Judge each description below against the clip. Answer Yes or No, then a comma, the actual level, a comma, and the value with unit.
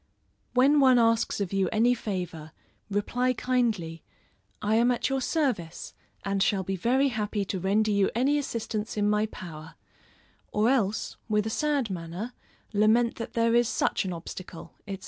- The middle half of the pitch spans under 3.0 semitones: No, average, 4.0 semitones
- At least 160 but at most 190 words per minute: Yes, average, 165 wpm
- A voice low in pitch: No, high, 215 Hz